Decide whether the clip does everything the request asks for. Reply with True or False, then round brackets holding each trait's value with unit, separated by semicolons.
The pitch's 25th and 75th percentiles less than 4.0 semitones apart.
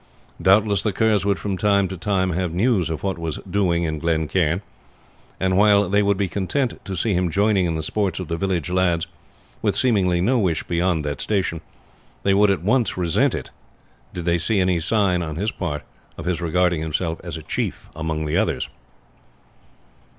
True (3.3 semitones)